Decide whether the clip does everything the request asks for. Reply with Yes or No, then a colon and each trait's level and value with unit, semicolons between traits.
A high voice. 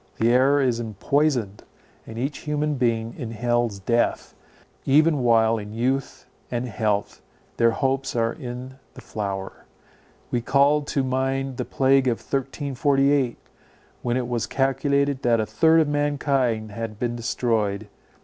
No: low, 125 Hz